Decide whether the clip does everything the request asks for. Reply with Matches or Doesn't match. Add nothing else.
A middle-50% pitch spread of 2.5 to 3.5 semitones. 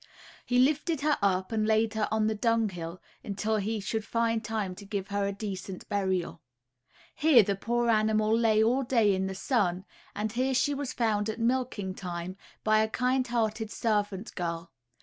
Matches